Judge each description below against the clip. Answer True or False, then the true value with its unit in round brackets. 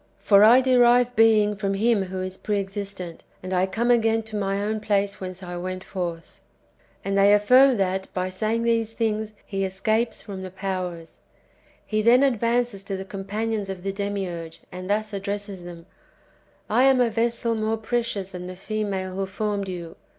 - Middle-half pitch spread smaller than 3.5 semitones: True (3.0 semitones)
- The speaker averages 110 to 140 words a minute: False (185 wpm)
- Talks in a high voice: True (200 Hz)